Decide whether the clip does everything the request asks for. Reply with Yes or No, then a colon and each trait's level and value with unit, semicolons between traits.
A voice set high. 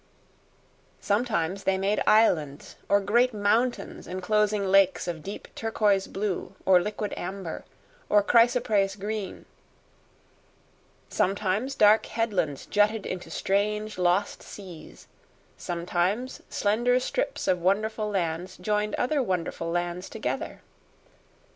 Yes: high, 200 Hz